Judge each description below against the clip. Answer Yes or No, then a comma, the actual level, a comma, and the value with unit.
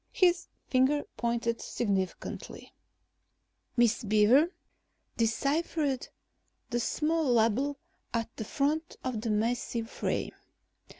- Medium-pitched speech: No, high, 240 Hz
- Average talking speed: No, slow, 95 wpm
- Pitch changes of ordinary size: Yes, average, 4.1 semitones